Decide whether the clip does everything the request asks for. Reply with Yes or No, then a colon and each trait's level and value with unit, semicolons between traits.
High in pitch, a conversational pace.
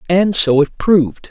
No: medium, 165 Hz; average, 185 wpm